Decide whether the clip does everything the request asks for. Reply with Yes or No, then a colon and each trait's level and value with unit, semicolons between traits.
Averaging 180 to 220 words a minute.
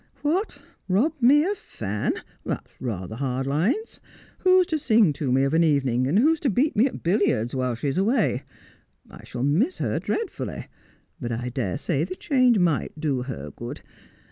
Yes: average, 185 wpm